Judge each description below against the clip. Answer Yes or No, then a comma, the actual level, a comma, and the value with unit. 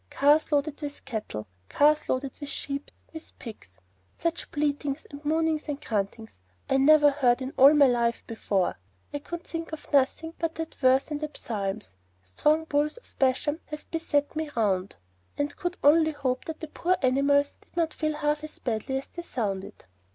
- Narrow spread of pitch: No, average, 3.3 semitones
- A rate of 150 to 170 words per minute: No, average, 180 wpm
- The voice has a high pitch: Yes, very high, 290 Hz